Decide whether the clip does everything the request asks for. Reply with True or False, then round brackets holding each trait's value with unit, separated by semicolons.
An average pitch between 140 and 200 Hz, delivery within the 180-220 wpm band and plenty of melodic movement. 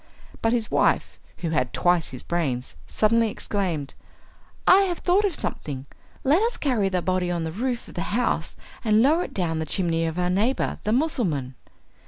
True (190 Hz; 185 wpm; 7.2 semitones)